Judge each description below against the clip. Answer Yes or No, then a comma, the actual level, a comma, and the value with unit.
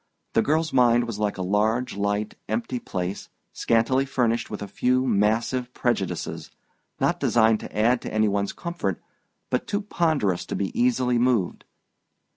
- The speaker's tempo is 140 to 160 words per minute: Yes, average, 155 wpm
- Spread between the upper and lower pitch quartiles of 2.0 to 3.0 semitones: No, average, 3.5 semitones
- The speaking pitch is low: Yes, low, 115 Hz